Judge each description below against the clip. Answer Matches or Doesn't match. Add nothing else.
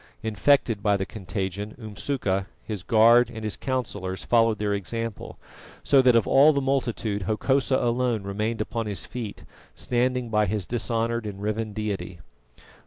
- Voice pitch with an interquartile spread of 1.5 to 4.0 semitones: Matches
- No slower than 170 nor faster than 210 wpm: Doesn't match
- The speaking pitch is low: Matches